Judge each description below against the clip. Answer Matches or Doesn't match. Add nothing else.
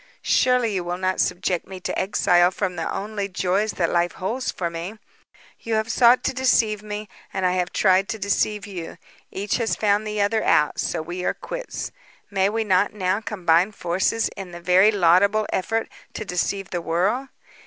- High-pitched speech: Matches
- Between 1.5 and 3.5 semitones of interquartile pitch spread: Matches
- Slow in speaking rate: Doesn't match